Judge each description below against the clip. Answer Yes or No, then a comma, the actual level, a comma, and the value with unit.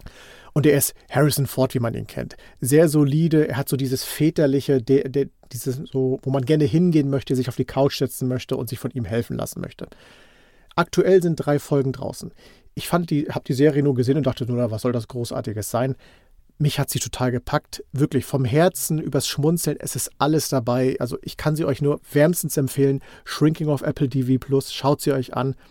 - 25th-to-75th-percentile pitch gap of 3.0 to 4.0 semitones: No, narrow, 2.4 semitones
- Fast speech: Yes, fast, 210 wpm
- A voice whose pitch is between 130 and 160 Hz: Yes, medium, 140 Hz